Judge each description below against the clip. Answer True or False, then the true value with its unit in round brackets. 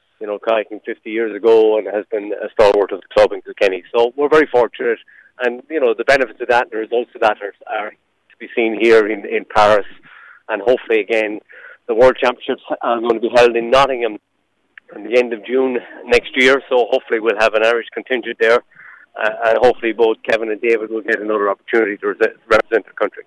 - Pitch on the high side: False (120 Hz)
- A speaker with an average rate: False (215 wpm)